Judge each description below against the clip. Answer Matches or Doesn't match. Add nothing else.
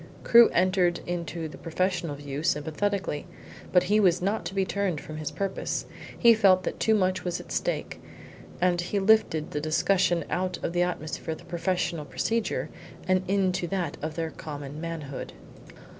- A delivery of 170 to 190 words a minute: Doesn't match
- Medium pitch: Matches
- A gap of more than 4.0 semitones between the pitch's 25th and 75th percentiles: Doesn't match